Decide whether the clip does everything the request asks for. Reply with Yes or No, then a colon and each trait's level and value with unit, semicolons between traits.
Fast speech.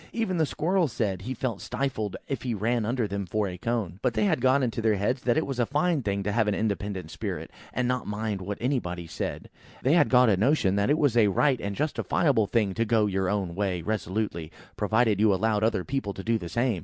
Yes: fast, 240 wpm